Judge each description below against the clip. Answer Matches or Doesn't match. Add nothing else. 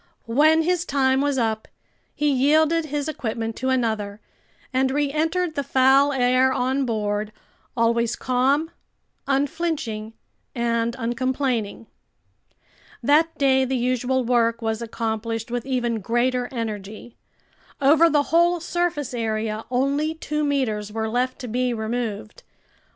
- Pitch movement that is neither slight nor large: Matches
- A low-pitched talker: Doesn't match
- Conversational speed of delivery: Doesn't match